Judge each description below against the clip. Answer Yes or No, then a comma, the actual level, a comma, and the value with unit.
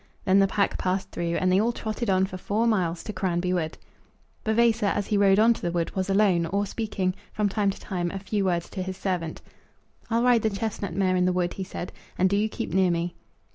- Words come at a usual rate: No, fast, 240 wpm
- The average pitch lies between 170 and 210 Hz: Yes, high, 190 Hz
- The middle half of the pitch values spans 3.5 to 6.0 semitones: No, narrow, 2.5 semitones